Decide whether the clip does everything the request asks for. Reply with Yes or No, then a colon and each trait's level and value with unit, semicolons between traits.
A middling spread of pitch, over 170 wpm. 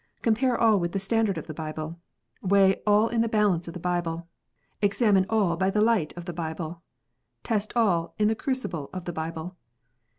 Yes: average, 4.3 semitones; average, 190 wpm